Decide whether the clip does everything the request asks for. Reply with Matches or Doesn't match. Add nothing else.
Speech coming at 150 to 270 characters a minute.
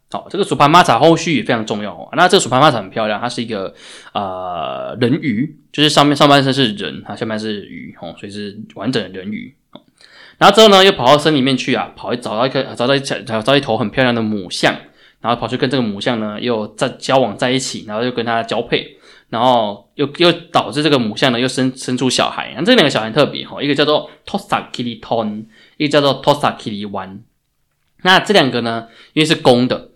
Doesn't match